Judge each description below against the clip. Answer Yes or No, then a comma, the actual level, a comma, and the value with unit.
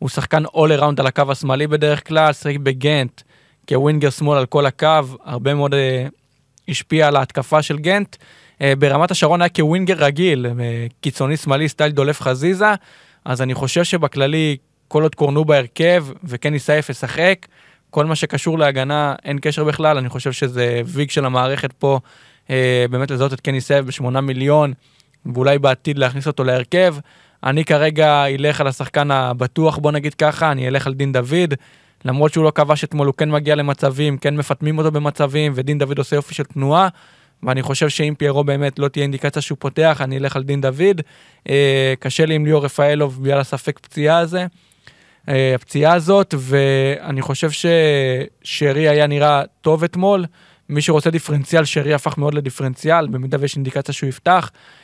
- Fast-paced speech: Yes, fast, 160 wpm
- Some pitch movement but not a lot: No, narrow, 2.1 semitones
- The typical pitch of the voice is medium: Yes, medium, 145 Hz